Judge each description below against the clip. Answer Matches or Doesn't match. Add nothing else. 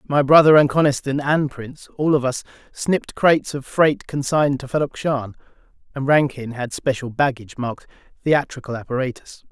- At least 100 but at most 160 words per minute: Matches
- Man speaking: Matches